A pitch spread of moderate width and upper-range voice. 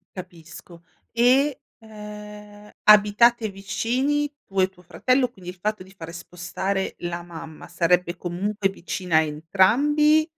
Yes: average, 4.6 semitones; high, 195 Hz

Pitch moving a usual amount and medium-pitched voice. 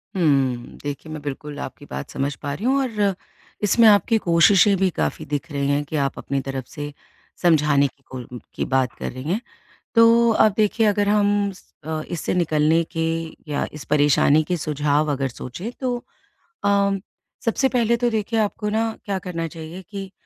No: wide, 6.1 semitones; medium, 170 Hz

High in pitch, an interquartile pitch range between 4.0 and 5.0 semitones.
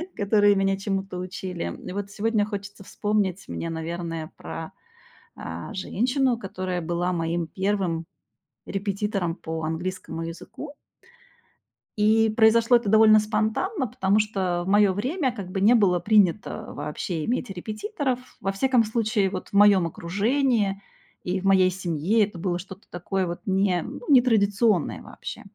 No: high, 195 Hz; average, 3.2 semitones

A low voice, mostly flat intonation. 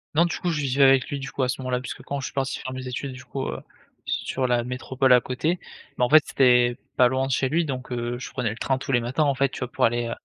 Yes: low, 130 Hz; narrow, 1.7 semitones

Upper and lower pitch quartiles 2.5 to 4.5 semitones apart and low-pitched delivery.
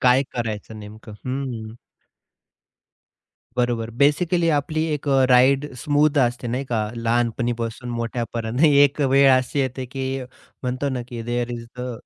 Yes: average, 2.9 semitones; low, 125 Hz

